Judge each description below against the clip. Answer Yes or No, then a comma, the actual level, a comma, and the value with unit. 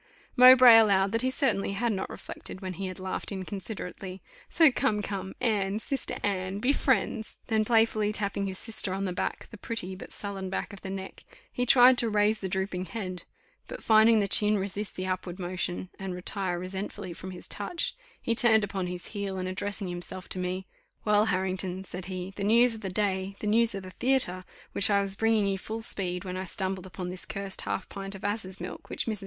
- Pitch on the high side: Yes, high, 195 Hz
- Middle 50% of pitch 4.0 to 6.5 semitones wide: No, average, 2.7 semitones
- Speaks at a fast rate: Yes, fast, 210 wpm